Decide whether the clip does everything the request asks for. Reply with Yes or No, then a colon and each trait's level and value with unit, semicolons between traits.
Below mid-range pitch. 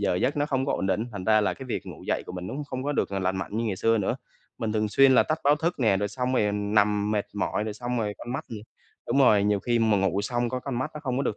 Yes: low, 110 Hz